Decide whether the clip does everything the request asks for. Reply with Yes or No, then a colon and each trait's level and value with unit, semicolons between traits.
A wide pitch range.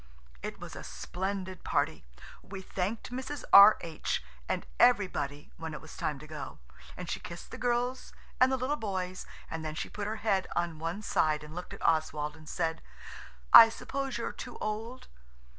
Yes: wide, 5.8 semitones